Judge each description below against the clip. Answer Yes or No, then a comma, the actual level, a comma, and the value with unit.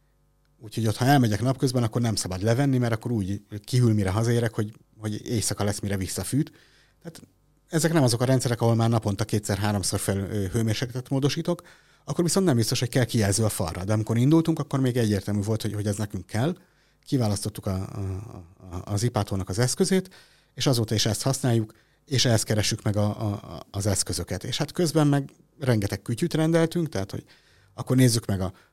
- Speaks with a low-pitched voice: Yes, low, 115 Hz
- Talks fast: Yes, fast, 185 wpm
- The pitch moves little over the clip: No, average, 4.9 semitones